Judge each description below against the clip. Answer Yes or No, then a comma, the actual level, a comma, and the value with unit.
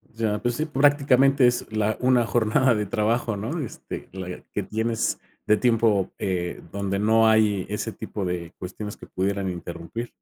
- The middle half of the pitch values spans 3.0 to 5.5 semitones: Yes, average, 3.3 semitones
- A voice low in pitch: Yes, low, 110 Hz